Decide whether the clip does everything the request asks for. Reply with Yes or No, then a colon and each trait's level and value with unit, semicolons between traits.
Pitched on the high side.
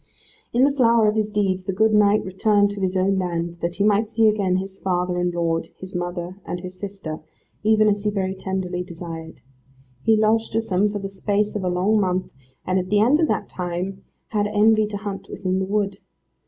Yes: high, 195 Hz